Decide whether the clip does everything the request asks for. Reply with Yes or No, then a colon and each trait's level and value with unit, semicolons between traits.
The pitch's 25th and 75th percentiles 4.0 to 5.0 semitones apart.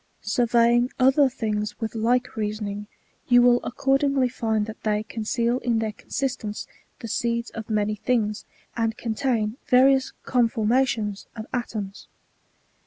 No: average, 2.7 semitones